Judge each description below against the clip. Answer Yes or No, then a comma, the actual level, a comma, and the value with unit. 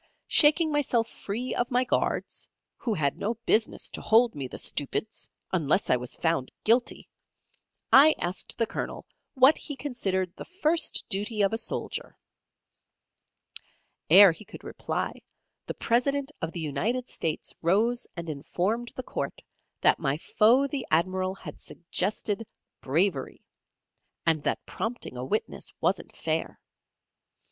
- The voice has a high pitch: Yes, high, 215 Hz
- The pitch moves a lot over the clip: Yes, wide, 6.6 semitones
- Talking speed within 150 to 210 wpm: No, slow, 135 wpm